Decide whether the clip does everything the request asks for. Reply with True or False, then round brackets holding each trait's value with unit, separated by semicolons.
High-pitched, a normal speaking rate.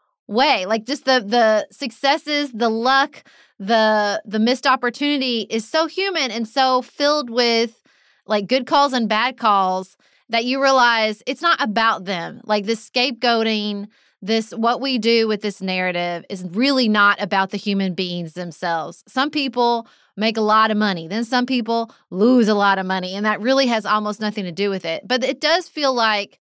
True (225 Hz; 180 wpm)